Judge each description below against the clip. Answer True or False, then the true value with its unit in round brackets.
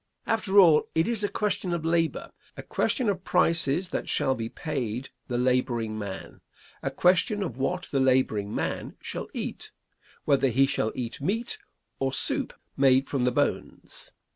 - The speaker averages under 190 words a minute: True (165 wpm)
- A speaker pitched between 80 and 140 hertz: True (135 Hz)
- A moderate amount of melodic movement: False (6.2 semitones)